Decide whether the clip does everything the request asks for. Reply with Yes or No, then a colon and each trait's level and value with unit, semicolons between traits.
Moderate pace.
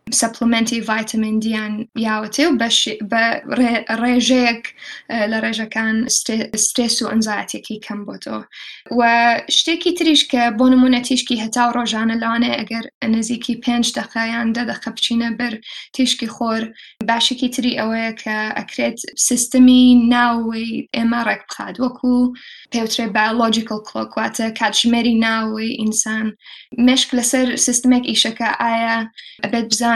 No: slow, 105 wpm